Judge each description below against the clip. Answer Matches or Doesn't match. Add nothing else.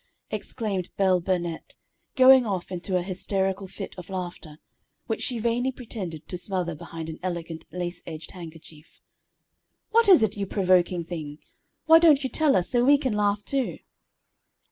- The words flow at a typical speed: Matches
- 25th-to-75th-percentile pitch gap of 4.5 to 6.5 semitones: Matches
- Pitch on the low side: Doesn't match